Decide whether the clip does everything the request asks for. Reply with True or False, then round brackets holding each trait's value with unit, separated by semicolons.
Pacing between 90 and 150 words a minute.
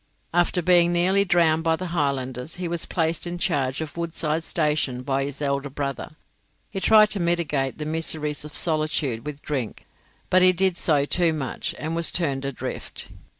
False (175 wpm)